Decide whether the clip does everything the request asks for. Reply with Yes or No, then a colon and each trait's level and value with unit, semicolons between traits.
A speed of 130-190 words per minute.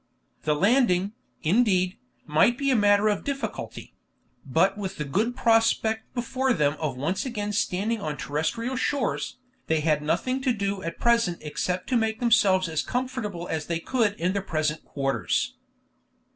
Yes: average, 160 wpm